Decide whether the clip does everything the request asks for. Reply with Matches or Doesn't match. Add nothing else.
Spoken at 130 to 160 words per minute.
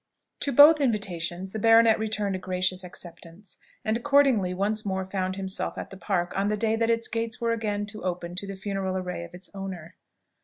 Doesn't match